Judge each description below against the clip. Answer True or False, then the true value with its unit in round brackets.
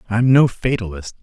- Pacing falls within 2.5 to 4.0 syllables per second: False (5.1 syllables/s)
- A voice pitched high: False (110 Hz)